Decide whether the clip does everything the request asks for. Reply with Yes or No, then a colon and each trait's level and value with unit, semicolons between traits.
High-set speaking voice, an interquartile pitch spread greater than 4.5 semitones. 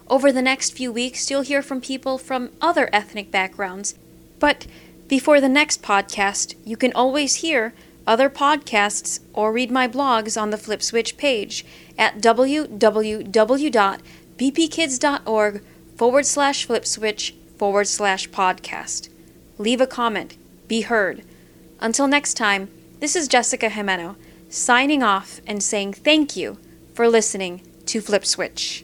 Yes: high, 225 Hz; average, 5.3 semitones